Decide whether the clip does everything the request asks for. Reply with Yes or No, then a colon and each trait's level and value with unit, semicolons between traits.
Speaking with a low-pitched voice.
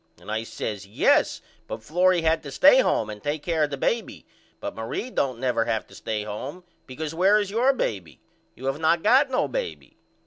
No: medium, 150 Hz